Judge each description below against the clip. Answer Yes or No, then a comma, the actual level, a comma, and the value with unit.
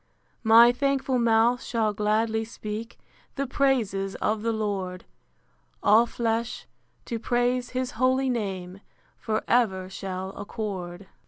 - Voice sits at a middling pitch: No, high, 225 Hz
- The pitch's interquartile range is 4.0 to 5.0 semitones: No, average, 3.3 semitones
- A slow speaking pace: Yes, slow, 115 wpm